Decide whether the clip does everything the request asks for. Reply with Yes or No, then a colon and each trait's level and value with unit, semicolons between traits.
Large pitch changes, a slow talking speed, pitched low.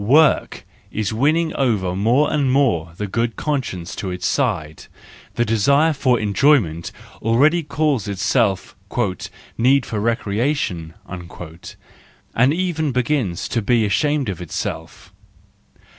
Yes: wide, 6.2 semitones; slow, 120 wpm; low, 120 Hz